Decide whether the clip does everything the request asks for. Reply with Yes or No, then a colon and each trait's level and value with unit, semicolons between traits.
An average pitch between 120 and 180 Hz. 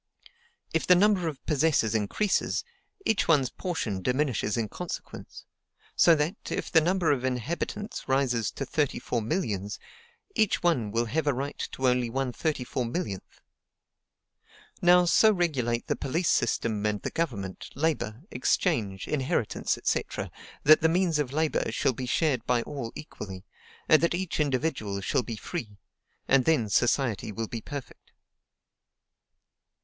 Yes: low, 135 Hz